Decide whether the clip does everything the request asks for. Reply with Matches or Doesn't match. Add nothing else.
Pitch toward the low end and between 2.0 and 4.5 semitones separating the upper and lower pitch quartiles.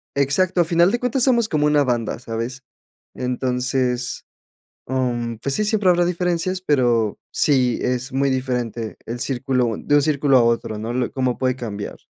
Matches